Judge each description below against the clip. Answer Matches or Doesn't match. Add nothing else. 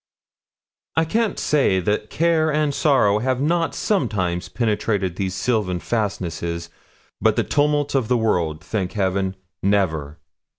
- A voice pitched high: Doesn't match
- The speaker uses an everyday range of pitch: Doesn't match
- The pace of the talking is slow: Matches